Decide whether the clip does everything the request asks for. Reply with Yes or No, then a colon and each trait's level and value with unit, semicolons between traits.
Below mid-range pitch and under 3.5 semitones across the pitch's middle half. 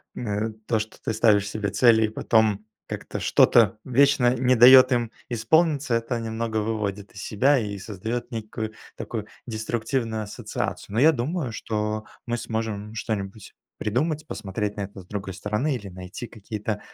Yes: low, 110 Hz; narrow, 2.6 semitones